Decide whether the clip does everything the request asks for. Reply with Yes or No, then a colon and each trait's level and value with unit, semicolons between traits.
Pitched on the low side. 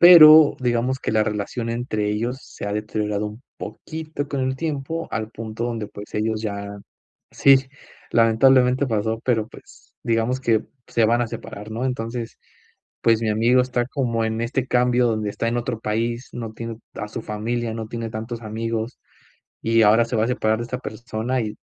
Yes: low, 115 Hz